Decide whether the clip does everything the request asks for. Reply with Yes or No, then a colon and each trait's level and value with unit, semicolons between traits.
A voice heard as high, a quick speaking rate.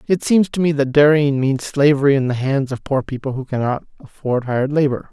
No: medium, 140 Hz; fast, 225 wpm